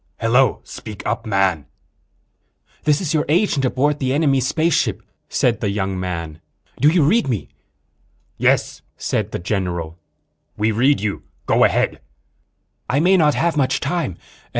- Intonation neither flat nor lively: No, wide, 7.3 semitones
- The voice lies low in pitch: Yes, low, 130 Hz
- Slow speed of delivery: No, average, 145 wpm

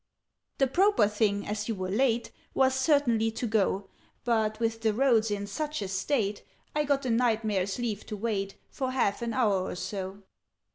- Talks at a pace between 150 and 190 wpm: Yes, average, 185 wpm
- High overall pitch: Yes, high, 225 Hz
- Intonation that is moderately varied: Yes, average, 4.0 semitones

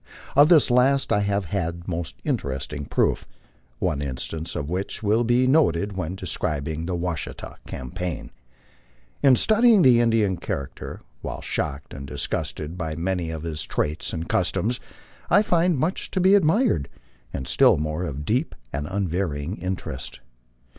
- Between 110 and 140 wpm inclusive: No, average, 150 wpm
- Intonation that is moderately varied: No, wide, 7.7 semitones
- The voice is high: No, very low, 90 Hz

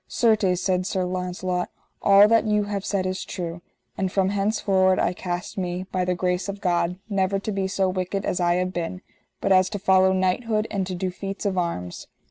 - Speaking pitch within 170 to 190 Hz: Yes, medium, 185 Hz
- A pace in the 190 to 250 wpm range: Yes, fast, 205 wpm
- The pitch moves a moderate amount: No, narrow, 1.6 semitones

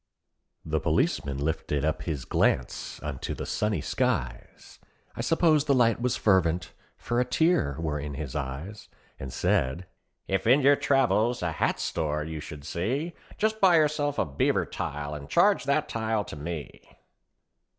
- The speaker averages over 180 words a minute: No, average, 160 wpm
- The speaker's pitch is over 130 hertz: No, very low, 90 Hz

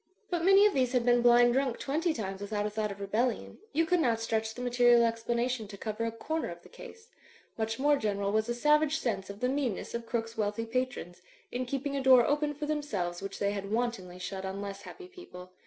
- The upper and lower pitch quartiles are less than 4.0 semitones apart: No, average, 4.9 semitones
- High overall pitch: Yes, high, 235 Hz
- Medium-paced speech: No, fast, 230 wpm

